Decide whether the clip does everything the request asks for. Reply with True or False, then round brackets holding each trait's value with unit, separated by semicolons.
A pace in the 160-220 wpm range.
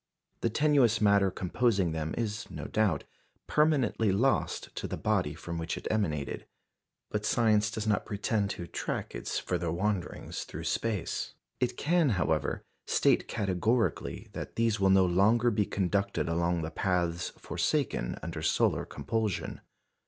False (145 wpm)